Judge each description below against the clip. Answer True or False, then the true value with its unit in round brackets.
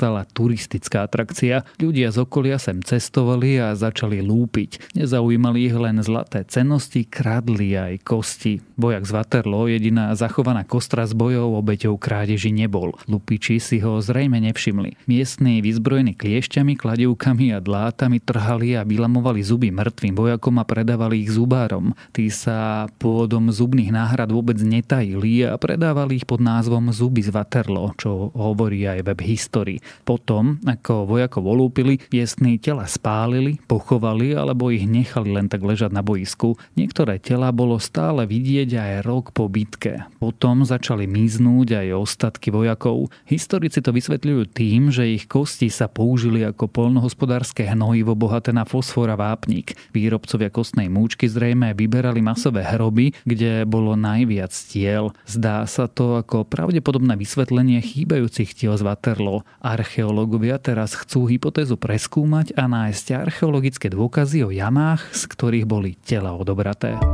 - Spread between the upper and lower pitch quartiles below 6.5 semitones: True (2.6 semitones)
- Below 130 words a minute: False (140 wpm)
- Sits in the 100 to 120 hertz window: True (115 Hz)